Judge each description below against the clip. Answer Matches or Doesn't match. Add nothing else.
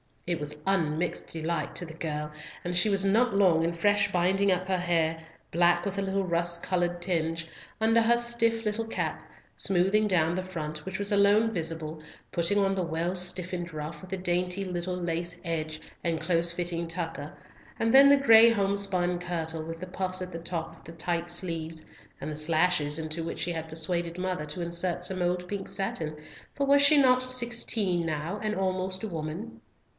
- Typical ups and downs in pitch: Matches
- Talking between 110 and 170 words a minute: Doesn't match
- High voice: Doesn't match